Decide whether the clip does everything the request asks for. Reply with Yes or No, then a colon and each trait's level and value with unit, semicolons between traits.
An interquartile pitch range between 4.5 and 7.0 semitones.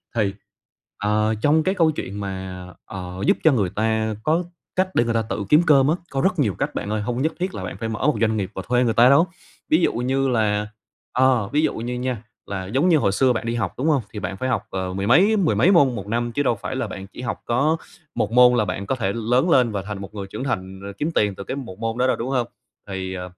Yes: average, 5.1 semitones